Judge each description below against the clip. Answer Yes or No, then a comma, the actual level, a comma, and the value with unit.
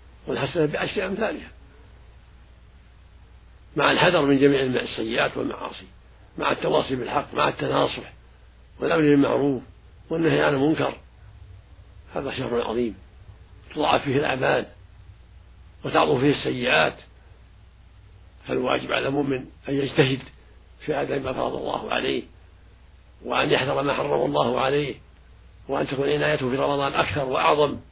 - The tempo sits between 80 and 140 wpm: Yes, average, 110 wpm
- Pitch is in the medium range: No, low, 105 Hz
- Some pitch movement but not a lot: No, wide, 7.5 semitones